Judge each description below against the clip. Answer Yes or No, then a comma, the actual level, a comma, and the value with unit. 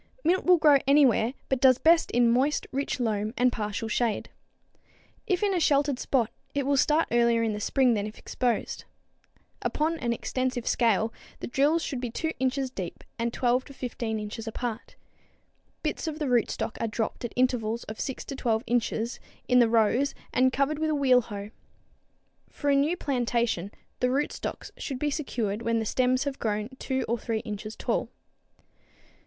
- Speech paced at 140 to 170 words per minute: No, average, 180 wpm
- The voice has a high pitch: Yes, very high, 250 Hz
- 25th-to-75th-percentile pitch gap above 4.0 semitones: No, average, 3.5 semitones